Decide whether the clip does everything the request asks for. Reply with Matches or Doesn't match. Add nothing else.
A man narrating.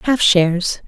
Doesn't match